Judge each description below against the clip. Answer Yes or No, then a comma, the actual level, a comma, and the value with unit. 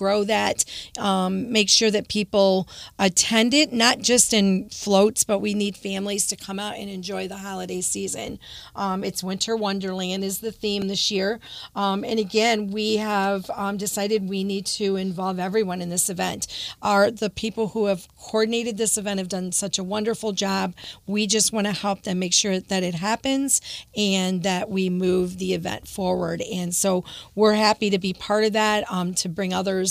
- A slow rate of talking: No, average, 190 wpm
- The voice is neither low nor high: No, high, 200 Hz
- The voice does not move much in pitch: Yes, narrow, 2.0 semitones